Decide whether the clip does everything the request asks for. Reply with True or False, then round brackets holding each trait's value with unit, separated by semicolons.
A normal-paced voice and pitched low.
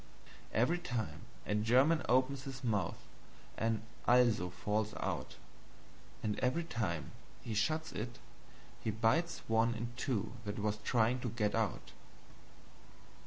False (125 wpm; 115 Hz)